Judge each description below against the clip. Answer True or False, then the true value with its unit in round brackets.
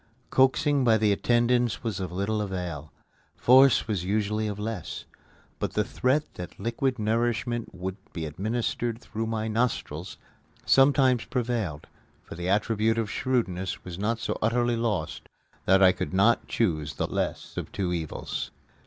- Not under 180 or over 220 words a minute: False (150 wpm)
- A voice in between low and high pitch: False (110 Hz)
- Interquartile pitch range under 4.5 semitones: True (3.9 semitones)